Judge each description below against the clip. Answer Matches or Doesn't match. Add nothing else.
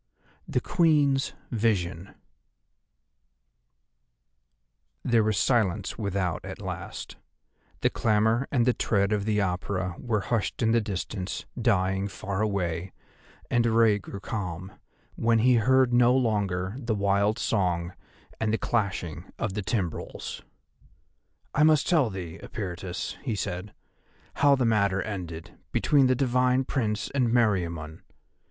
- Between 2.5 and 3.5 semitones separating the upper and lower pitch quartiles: Doesn't match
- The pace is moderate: Doesn't match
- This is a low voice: Matches